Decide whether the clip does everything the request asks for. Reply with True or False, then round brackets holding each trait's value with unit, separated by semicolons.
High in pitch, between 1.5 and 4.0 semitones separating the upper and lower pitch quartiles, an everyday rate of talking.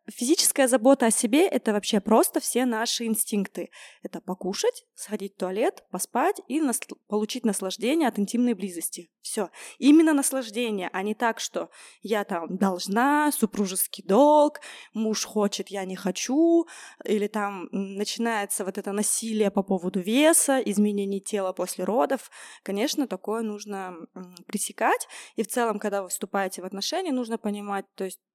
False (215 Hz; 4.8 semitones; 145 wpm)